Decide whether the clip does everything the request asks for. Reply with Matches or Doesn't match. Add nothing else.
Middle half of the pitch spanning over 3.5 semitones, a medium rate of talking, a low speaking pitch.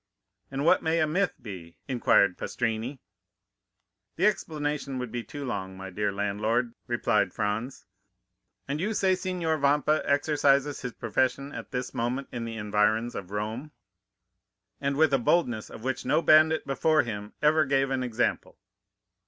Matches